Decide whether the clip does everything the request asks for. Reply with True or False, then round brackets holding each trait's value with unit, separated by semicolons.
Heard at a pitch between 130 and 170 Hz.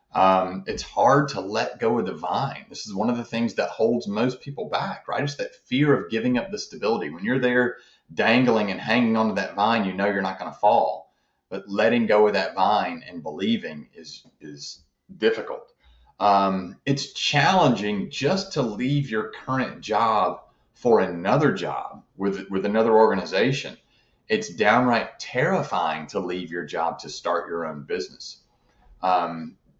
False (105 Hz)